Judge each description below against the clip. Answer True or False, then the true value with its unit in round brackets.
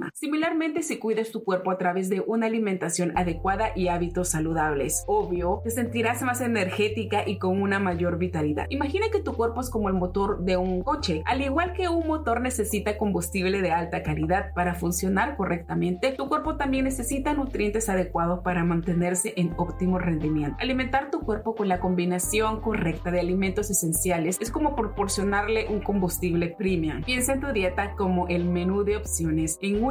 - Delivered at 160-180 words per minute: True (175 wpm)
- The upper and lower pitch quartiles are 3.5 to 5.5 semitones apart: True (4.3 semitones)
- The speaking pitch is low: False (195 Hz)